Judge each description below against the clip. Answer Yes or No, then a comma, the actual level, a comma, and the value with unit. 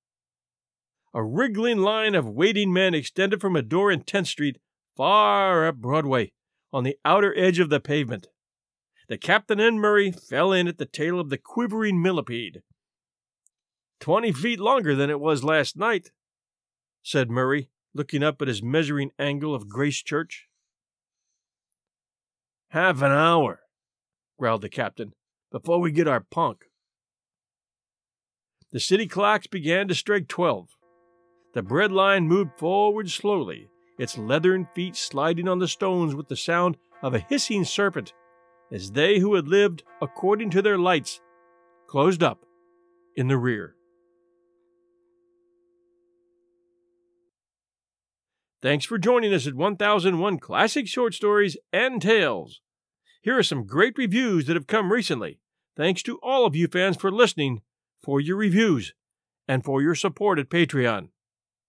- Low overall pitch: No, medium, 175 Hz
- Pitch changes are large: Yes, wide, 6.4 semitones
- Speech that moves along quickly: No, average, 140 wpm